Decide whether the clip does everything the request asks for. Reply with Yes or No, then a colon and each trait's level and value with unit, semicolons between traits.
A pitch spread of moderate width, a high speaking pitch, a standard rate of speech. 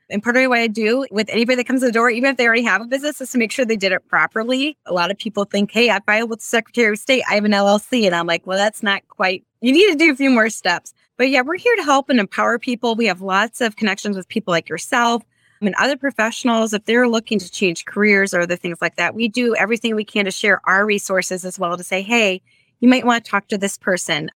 No: average, 4.1 semitones; high, 220 Hz; fast, 285 wpm